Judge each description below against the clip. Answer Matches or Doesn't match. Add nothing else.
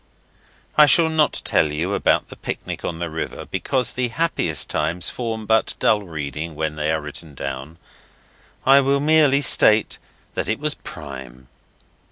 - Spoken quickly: Doesn't match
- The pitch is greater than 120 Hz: Doesn't match